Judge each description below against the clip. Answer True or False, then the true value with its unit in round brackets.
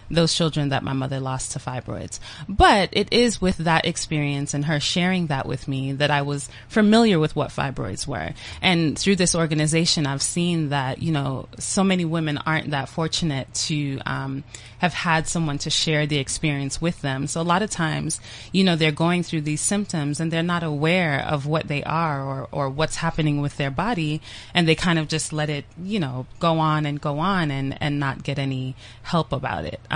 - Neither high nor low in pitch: True (155 Hz)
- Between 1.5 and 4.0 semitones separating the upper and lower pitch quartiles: True (3.3 semitones)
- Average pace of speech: False (210 wpm)